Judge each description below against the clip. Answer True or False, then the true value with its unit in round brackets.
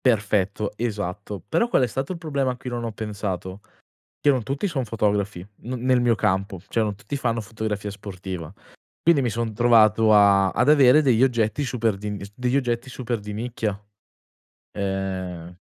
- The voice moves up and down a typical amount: True (3.7 semitones)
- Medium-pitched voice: False (110 Hz)